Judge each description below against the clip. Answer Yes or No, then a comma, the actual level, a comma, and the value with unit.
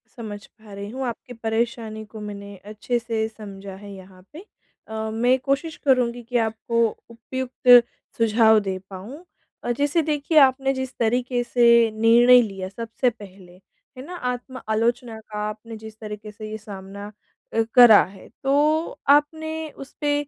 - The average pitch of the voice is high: Yes, high, 230 Hz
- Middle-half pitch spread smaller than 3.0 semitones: No, average, 3.4 semitones